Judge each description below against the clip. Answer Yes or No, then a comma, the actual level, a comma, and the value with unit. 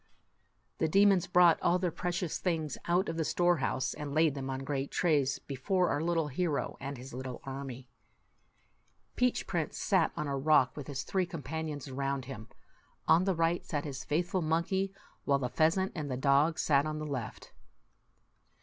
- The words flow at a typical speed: Yes, average, 175 wpm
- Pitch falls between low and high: Yes, medium, 150 Hz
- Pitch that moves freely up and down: No, average, 4.0 semitones